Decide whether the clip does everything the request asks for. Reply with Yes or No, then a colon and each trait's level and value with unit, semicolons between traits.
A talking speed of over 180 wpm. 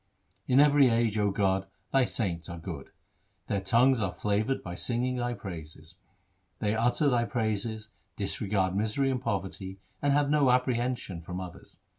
No: average, 155 wpm